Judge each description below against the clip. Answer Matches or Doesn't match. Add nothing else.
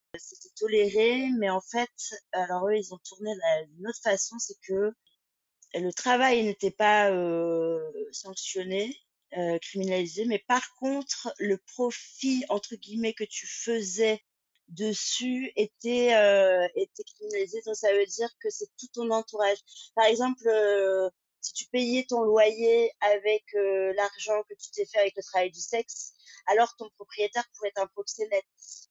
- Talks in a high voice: Matches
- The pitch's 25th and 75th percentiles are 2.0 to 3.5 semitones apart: Doesn't match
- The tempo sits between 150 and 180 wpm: Matches